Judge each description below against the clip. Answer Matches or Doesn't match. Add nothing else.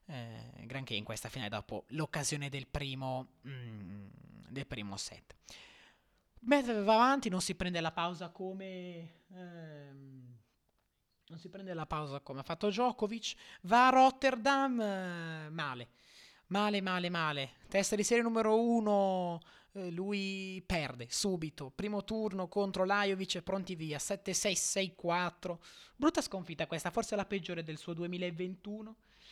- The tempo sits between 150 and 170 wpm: Doesn't match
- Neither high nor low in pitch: Matches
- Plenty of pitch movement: Matches